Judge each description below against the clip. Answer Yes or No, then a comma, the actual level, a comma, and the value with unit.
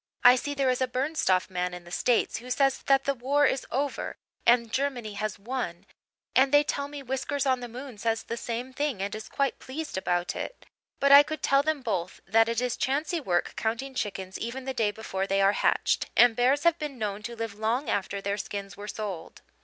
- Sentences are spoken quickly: Yes, fast, 220 wpm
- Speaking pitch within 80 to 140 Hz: No, high, 245 Hz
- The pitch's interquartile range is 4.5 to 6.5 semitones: Yes, average, 5.0 semitones